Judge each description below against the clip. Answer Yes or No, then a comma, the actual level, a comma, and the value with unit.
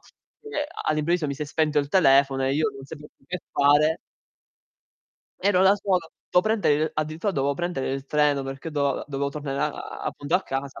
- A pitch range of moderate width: Yes, average, 3.7 semitones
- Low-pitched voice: No, medium, 150 Hz